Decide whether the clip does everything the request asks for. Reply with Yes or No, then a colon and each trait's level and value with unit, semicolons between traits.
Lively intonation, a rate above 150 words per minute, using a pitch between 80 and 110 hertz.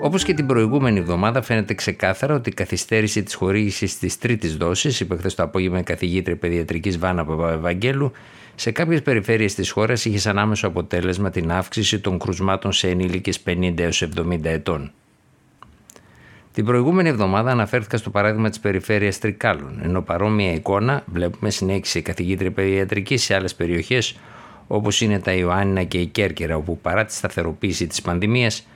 No: average, 3.5 semitones; average, 160 wpm; low, 100 Hz